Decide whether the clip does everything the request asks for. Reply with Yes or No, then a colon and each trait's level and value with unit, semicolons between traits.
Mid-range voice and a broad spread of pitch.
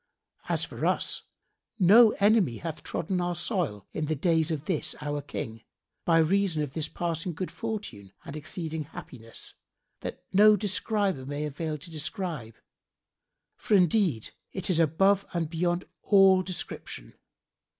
No: medium, 165 Hz; average, 4.2 semitones